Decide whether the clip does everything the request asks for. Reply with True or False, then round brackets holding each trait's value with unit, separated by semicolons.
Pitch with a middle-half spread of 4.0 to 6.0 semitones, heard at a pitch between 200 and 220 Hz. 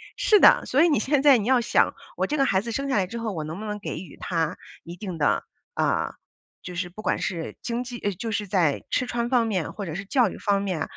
True (5.0 semitones; 210 Hz)